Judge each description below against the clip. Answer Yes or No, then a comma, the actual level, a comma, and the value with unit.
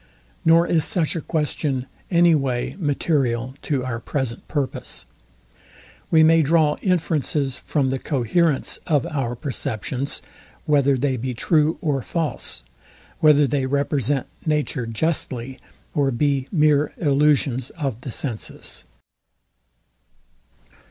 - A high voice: No, medium, 140 Hz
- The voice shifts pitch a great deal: No, average, 3.0 semitones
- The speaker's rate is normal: No, slow, 115 wpm